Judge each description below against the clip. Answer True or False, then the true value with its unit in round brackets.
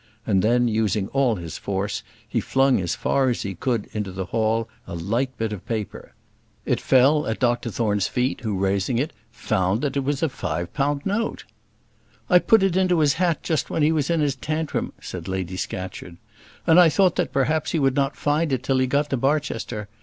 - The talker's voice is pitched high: False (130 Hz)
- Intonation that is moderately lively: False (6.1 semitones)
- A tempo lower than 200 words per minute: False (205 wpm)